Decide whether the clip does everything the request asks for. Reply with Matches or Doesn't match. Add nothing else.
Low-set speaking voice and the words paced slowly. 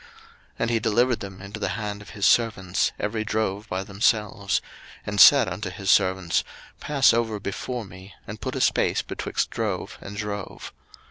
Doesn't match